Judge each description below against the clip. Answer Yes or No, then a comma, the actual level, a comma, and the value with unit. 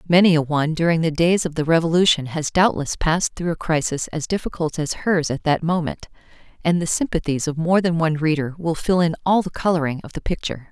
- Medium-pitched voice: Yes, medium, 165 Hz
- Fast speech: Yes, fast, 220 wpm